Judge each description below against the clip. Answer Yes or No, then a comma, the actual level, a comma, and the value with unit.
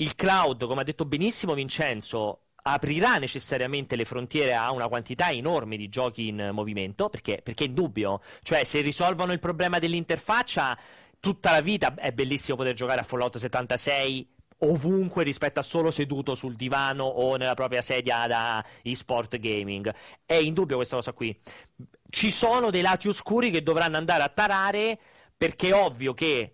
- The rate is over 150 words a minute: Yes, average, 165 wpm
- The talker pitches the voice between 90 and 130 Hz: No, medium, 140 Hz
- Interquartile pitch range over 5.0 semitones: Yes, wide, 5.5 semitones